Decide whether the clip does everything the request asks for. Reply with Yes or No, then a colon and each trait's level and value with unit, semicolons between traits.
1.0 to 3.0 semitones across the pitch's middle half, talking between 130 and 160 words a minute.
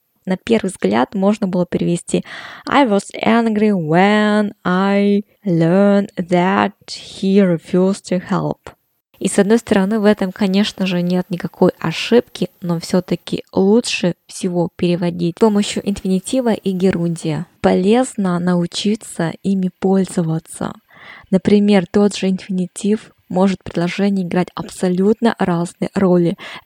No: narrow, 2.4 semitones; average, 120 wpm